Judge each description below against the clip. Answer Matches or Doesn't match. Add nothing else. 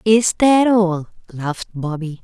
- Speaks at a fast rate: Doesn't match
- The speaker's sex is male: Doesn't match